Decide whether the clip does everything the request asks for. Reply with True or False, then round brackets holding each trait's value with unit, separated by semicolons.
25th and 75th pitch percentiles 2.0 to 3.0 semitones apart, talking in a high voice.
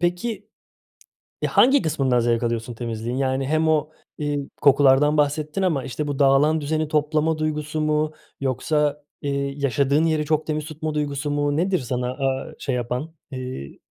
False (2.7 semitones; 145 Hz)